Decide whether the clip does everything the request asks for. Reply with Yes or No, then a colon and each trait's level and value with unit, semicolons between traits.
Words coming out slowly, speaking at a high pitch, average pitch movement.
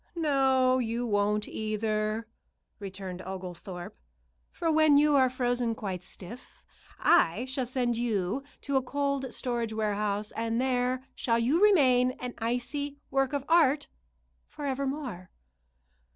Yes: slow, 125 wpm; high, 245 Hz; average, 4.2 semitones